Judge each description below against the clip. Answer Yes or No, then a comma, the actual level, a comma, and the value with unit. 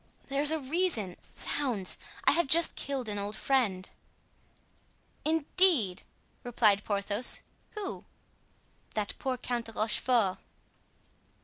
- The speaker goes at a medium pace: No, slow, 105 wpm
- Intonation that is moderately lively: No, wide, 6.1 semitones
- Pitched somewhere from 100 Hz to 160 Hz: No, high, 245 Hz